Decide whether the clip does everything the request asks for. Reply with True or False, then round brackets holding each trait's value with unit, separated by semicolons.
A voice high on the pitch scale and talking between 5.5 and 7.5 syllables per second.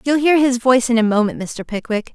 True (240 Hz; 5.9 syllables/s)